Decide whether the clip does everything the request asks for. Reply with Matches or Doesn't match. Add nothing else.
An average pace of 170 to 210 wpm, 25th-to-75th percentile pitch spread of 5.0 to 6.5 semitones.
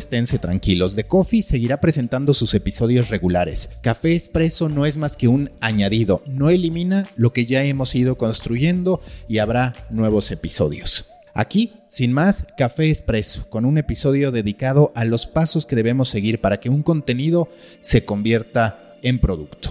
Doesn't match